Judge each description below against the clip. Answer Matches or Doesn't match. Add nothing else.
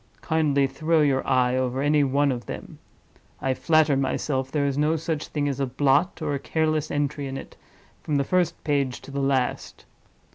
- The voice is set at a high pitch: Doesn't match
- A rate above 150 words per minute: Matches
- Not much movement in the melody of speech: Matches